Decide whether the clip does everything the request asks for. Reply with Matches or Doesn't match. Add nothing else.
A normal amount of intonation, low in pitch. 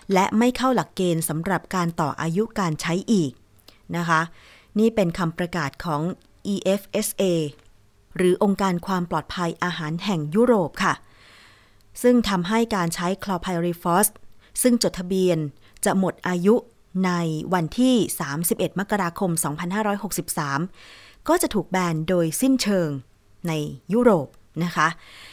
Doesn't match